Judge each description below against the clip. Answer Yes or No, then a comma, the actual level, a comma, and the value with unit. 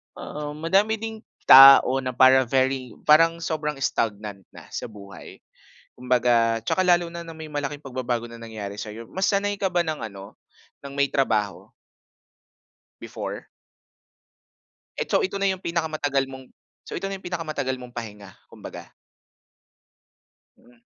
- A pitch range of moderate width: No, wide, 5.9 semitones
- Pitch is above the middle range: No, low, 135 Hz